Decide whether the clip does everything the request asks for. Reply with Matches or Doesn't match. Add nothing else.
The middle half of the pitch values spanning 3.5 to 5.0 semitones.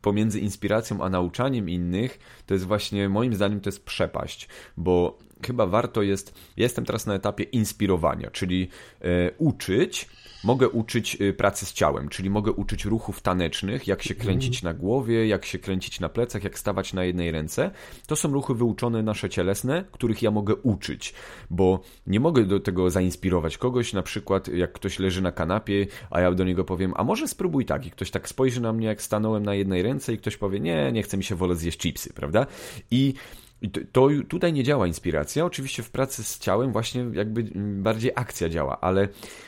Matches